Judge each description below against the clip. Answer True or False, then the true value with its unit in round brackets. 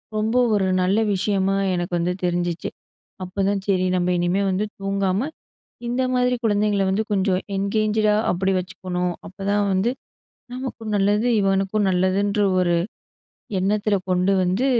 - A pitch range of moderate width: False (2.3 semitones)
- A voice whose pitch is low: False (195 Hz)